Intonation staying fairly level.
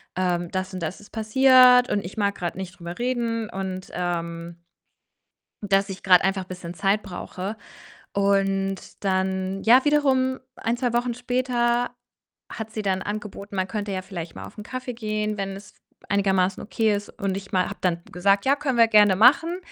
No: average, 3.9 semitones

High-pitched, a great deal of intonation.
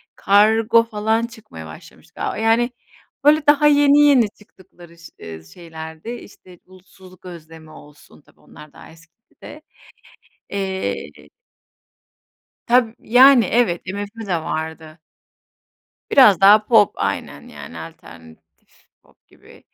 Yes: high, 195 Hz; wide, 6.3 semitones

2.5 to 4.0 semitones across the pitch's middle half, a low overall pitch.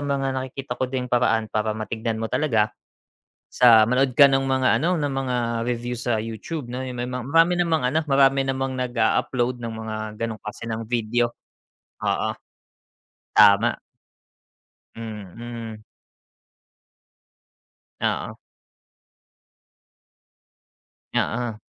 Yes: average, 3.0 semitones; low, 125 Hz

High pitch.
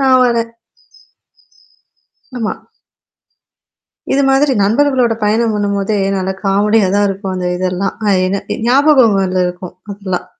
Yes: high, 205 Hz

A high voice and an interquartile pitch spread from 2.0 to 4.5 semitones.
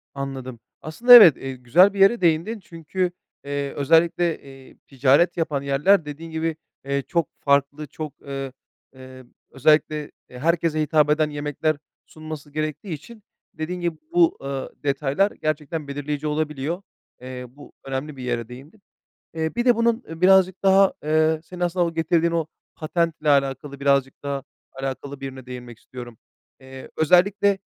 No: medium, 155 Hz; average, 3.7 semitones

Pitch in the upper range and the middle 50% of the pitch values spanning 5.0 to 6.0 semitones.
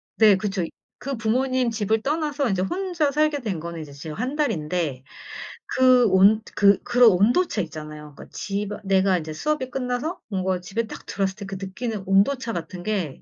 Yes: high, 210 Hz; wide, 5.6 semitones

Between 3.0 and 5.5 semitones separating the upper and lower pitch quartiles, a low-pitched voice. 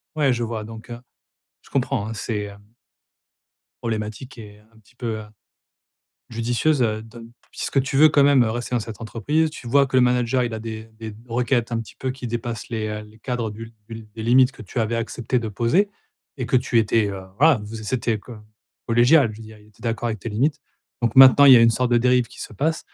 No: narrow, 2.5 semitones; low, 115 Hz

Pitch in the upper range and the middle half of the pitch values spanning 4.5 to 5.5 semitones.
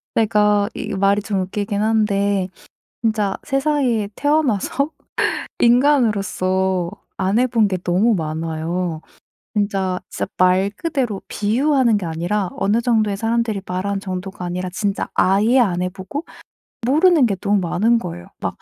No: high, 205 Hz; average, 3.9 semitones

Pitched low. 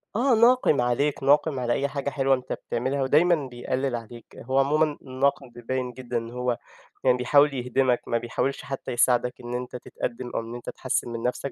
Yes: low, 130 Hz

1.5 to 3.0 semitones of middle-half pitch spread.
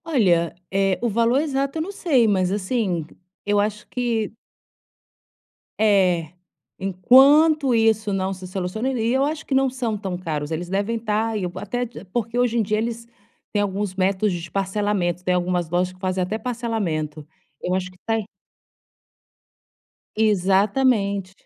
No: average, 4.2 semitones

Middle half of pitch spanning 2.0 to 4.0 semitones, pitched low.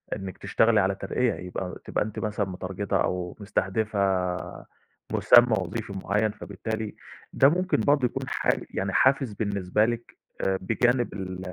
Yes: average, 3.4 semitones; low, 105 Hz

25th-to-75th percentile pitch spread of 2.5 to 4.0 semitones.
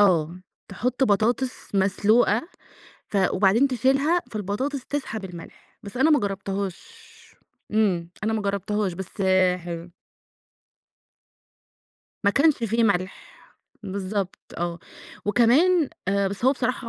No: average, 4.8 semitones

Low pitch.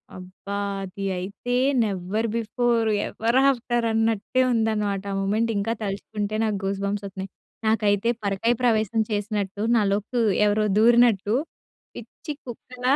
No: high, 215 Hz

